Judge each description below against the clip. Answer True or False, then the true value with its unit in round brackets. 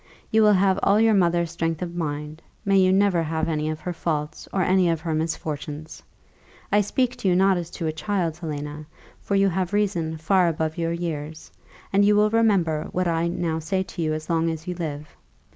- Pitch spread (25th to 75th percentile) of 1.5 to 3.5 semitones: True (3.2 semitones)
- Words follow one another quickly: True (210 wpm)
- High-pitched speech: False (170 Hz)